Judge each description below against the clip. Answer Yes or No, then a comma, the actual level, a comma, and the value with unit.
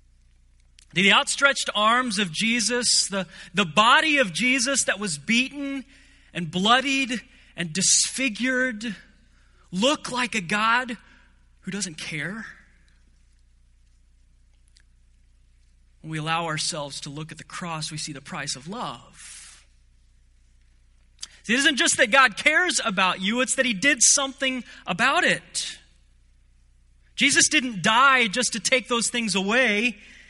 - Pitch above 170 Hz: Yes, high, 190 Hz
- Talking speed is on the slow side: Yes, slow, 125 wpm